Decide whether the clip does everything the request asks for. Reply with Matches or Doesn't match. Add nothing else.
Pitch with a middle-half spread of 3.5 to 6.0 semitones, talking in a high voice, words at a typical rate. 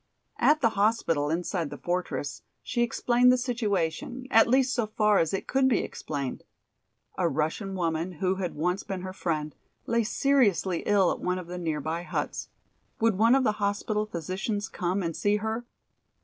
Matches